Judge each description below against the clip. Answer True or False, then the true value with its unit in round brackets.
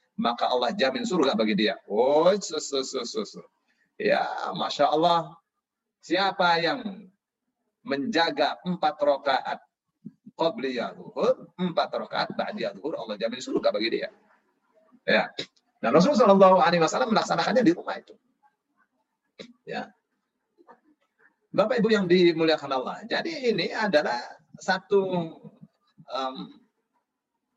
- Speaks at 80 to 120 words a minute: True (105 wpm)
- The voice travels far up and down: True (6.2 semitones)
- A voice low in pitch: False (195 Hz)